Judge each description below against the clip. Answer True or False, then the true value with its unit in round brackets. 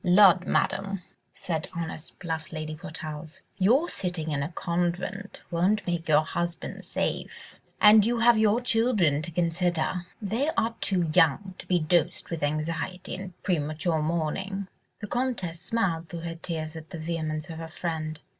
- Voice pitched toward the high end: False (170 Hz)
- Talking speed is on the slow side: False (155 wpm)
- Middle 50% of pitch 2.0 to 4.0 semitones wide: True (3.4 semitones)